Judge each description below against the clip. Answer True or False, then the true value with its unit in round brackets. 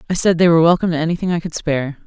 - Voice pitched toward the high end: False (165 Hz)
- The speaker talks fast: True (290 wpm)